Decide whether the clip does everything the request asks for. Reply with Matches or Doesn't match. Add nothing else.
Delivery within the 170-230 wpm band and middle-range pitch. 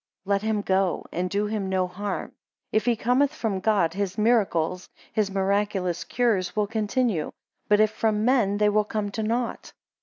Doesn't match